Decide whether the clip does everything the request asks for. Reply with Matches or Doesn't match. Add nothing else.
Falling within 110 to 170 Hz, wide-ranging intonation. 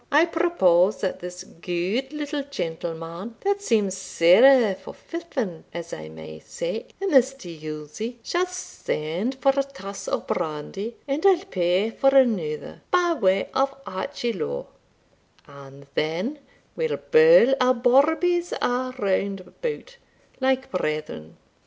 Doesn't match